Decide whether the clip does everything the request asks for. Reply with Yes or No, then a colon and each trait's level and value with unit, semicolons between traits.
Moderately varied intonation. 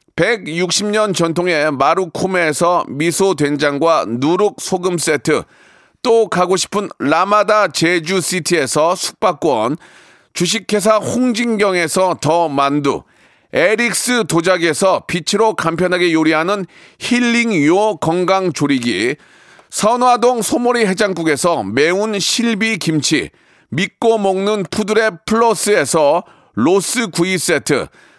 Yes: average, 4.4 semitones